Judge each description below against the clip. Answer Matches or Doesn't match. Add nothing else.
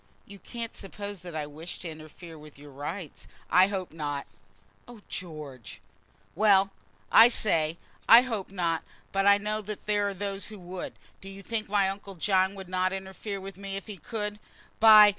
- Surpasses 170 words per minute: Matches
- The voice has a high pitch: Matches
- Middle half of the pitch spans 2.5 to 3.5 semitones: Matches